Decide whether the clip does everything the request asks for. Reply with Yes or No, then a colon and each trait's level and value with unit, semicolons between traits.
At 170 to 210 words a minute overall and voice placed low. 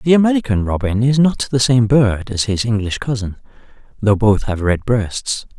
Yes: average, 185 wpm; low, 115 Hz